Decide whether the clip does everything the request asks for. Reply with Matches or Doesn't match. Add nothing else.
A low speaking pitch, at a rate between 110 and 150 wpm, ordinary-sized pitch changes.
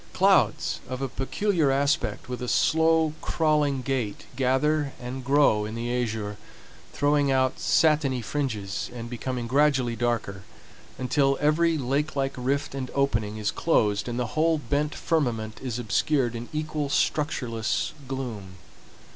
Matches